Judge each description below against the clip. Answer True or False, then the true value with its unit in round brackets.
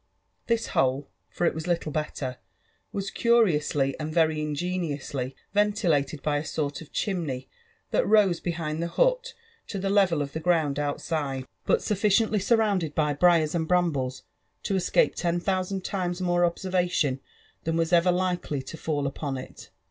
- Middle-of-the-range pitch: True (170 Hz)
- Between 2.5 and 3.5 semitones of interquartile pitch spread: False (4.1 semitones)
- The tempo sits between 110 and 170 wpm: True (160 wpm)